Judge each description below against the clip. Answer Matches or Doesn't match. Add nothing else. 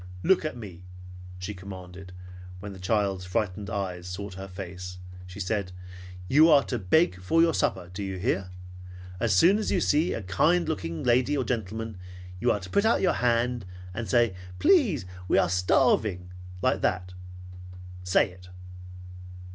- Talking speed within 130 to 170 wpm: Matches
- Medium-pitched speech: Doesn't match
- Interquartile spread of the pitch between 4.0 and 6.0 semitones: Matches